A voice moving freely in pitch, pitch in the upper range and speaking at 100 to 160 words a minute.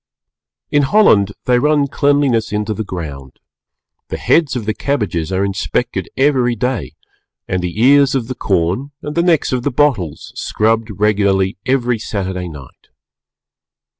No: wide, 6.1 semitones; low, 115 Hz; average, 145 wpm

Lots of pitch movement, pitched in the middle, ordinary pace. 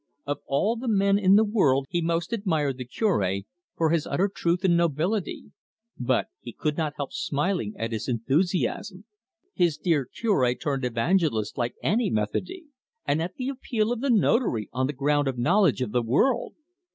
Yes: wide, 7.3 semitones; medium, 160 Hz; average, 175 wpm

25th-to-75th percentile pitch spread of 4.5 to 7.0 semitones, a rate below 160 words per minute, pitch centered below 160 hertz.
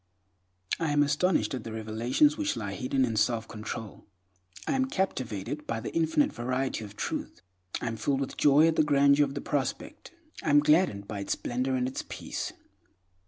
No: average, 4.8 semitones; average, 185 wpm; low, 135 Hz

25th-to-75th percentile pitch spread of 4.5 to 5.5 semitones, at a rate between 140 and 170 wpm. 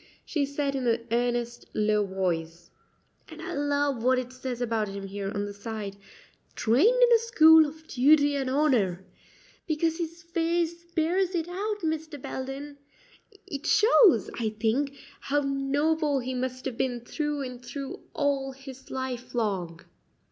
Yes: average, 4.8 semitones; average, 155 wpm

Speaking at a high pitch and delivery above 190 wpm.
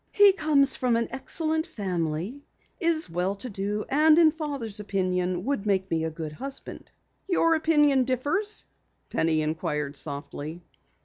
No: high, 230 Hz; average, 140 wpm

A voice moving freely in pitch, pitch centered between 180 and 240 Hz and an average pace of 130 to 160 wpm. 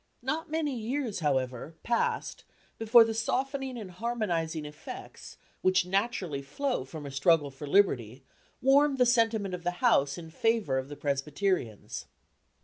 Yes: wide, 8.5 semitones; medium, 185 Hz; average, 140 wpm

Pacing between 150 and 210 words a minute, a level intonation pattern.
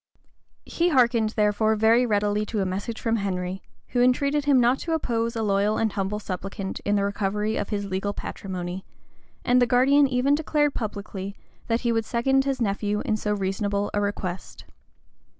No: average, 175 wpm; average, 3.5 semitones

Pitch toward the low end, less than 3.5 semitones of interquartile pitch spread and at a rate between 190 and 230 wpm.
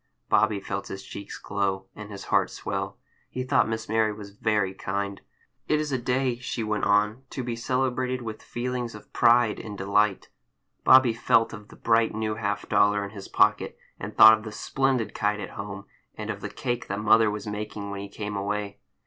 Yes: low, 105 Hz; narrow, 2.6 semitones; average, 200 wpm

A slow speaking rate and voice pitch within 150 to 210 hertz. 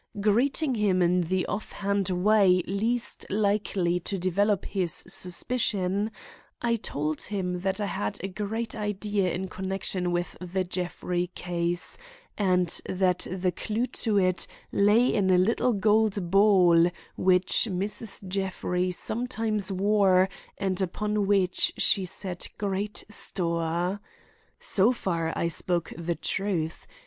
Yes: slow, 125 wpm; high, 190 Hz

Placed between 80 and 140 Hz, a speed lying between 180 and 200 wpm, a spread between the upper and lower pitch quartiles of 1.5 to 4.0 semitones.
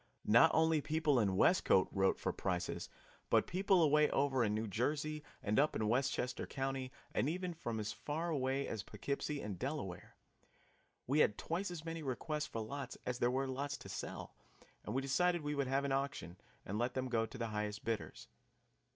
No: low, 135 Hz; average, 190 wpm; average, 5.3 semitones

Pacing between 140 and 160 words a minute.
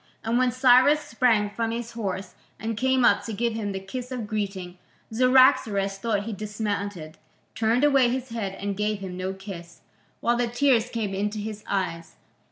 No: average, 175 wpm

